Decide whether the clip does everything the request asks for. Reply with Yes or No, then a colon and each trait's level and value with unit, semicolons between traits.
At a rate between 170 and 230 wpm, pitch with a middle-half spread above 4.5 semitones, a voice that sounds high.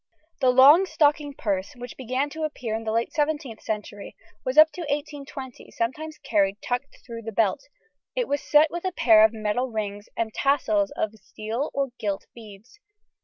Yes: average, 175 wpm; average, 5.2 semitones; very high, 250 Hz